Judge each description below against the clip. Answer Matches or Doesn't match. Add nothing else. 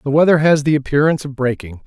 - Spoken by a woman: Doesn't match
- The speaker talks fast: Matches